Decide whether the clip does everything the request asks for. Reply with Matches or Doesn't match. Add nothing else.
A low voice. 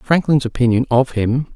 Matches